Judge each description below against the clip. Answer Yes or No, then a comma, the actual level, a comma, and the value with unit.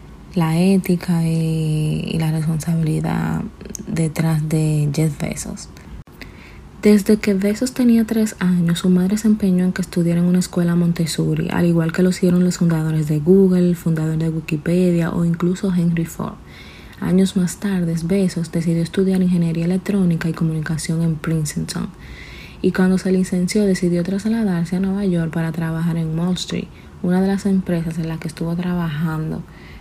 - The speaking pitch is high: No, medium, 170 Hz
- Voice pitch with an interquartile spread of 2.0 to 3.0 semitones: Yes, narrow, 2.5 semitones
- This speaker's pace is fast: No, average, 160 wpm